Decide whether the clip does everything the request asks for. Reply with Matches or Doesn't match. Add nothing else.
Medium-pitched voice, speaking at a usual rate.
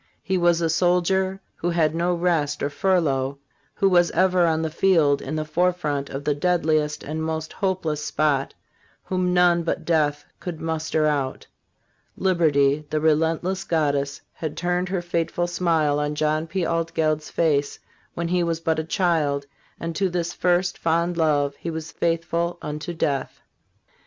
Matches